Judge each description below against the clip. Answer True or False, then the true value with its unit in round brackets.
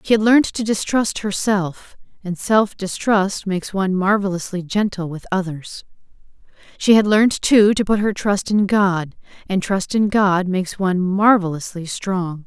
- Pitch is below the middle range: False (195 Hz)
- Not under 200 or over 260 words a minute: False (160 wpm)